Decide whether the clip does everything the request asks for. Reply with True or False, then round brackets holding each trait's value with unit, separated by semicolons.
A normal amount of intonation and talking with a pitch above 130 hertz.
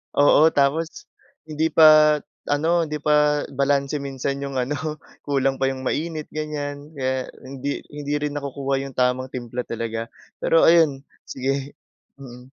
False (2.0 semitones; 140 Hz)